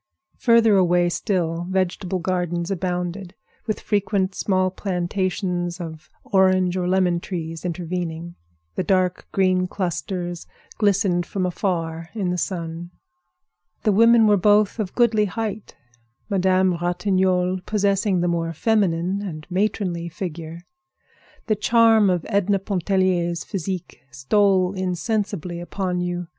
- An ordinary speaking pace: No, slow, 120 wpm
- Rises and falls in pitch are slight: Yes, narrow, 2.3 semitones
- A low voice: No, medium, 185 Hz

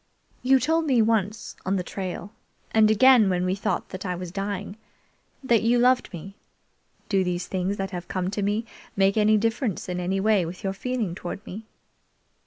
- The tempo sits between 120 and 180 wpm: No, average, 190 wpm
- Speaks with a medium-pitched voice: No, high, 200 Hz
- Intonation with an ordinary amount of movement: Yes, average, 3.3 semitones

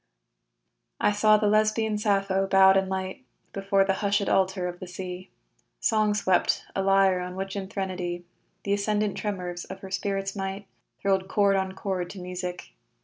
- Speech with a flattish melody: Yes, narrow, 1.3 semitones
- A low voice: No, high, 195 Hz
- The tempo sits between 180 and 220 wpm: No, average, 165 wpm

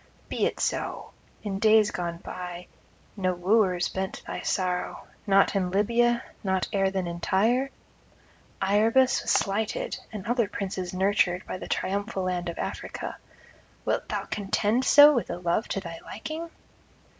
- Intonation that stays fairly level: No, average, 3.3 semitones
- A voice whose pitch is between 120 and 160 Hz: No, high, 195 Hz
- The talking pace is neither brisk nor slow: Yes, average, 150 wpm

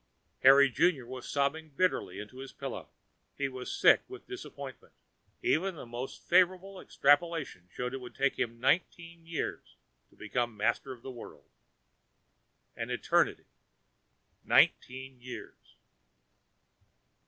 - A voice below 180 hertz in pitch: Yes, low, 135 Hz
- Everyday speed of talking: No, slow, 120 wpm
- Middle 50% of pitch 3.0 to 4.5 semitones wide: No, average, 5.1 semitones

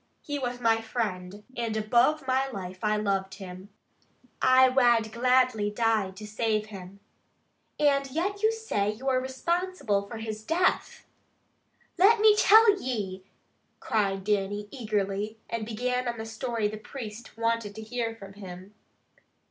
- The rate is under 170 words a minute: Yes, average, 150 wpm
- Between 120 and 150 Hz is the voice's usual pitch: No, high, 225 Hz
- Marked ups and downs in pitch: No, average, 3.8 semitones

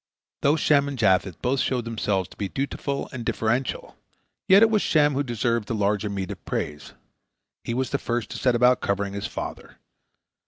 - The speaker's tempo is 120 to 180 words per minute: No, average, 190 wpm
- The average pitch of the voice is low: Yes, low, 120 Hz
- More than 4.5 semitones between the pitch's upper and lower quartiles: Yes, average, 5.2 semitones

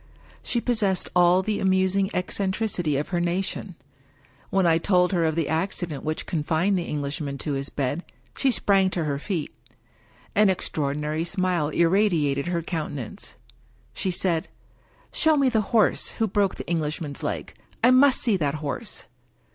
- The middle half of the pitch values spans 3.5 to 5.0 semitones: Yes, average, 4.2 semitones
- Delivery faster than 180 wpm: No, average, 155 wpm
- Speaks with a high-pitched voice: No, medium, 175 Hz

